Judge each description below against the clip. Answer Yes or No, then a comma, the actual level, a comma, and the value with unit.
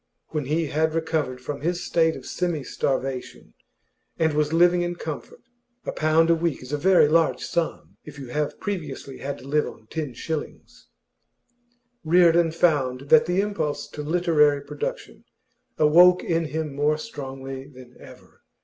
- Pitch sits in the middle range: Yes, medium, 155 Hz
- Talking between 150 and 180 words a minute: Yes, average, 160 wpm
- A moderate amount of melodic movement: Yes, average, 3.1 semitones